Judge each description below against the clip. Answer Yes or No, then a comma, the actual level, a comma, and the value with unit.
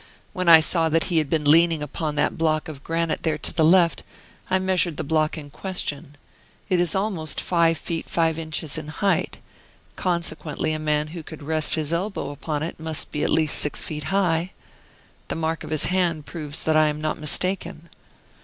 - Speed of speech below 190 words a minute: No, average, 195 wpm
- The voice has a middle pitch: Yes, medium, 160 Hz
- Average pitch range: No, narrow, 1.8 semitones